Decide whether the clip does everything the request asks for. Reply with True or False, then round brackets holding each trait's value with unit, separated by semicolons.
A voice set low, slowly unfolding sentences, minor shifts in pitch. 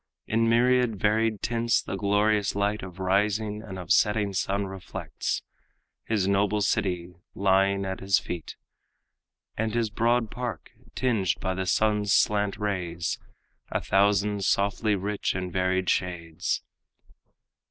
True (100 Hz; 130 wpm; 2.2 semitones)